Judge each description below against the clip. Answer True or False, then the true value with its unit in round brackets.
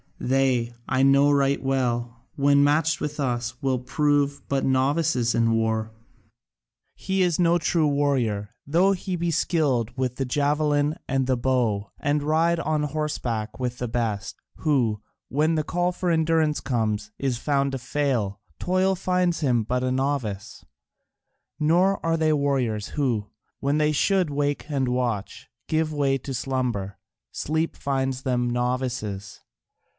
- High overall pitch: False (135 Hz)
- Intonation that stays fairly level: False (3.9 semitones)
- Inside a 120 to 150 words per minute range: True (145 wpm)